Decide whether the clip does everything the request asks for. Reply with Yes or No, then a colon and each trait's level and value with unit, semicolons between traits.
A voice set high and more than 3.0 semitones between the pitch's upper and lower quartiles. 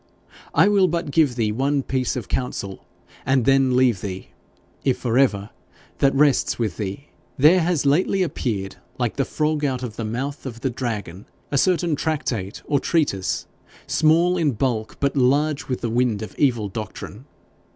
No: low, 130 Hz; average, 4.7 semitones